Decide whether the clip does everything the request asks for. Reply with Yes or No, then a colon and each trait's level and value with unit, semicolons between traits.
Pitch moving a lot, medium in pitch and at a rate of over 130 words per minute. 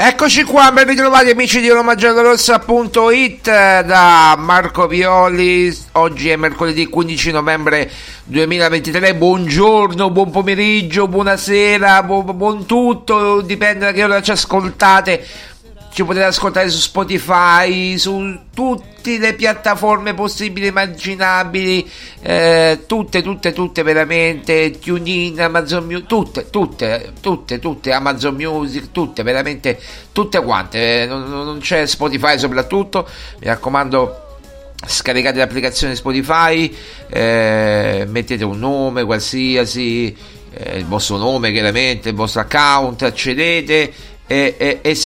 No: wide, 6.0 semitones; medium, 175 Hz; average, 120 wpm